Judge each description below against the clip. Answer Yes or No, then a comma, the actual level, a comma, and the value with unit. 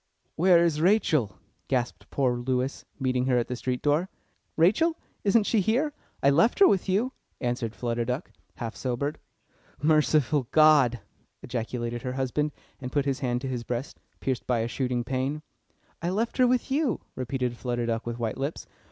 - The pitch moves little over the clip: No, average, 5.1 semitones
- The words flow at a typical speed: Yes, average, 170 wpm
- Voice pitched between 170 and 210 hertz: No, low, 135 Hz